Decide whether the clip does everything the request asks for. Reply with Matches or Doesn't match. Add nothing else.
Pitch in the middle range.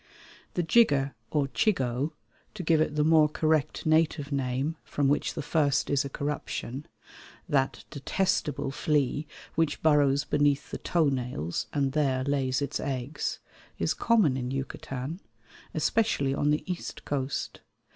Matches